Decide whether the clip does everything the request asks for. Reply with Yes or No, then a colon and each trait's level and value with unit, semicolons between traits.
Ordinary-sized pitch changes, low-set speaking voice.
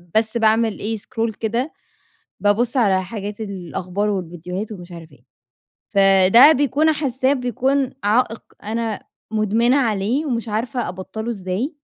No: average, 3.9 semitones; high, 220 Hz